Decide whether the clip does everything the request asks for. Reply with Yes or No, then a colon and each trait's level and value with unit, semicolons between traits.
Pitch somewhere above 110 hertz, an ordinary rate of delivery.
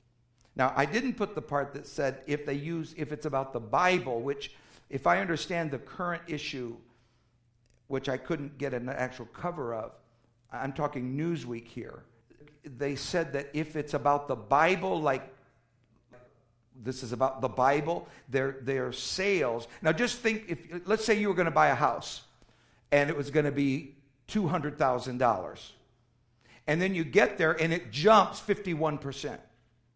Yes: medium, 140 Hz; average, 160 wpm